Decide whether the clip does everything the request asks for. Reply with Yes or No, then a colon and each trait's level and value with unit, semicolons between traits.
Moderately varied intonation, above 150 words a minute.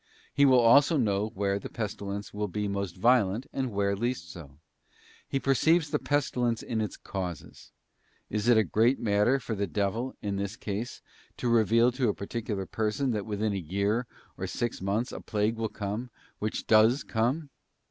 Yes: average, 3.4 semitones; average, 180 wpm